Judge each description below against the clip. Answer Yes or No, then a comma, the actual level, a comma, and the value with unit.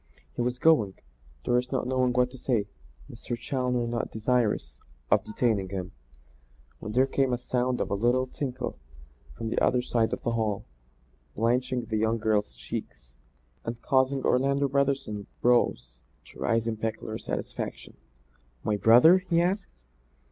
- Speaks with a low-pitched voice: Yes, low, 120 Hz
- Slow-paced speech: No, average, 150 wpm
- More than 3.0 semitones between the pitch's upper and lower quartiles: No, average, 2.7 semitones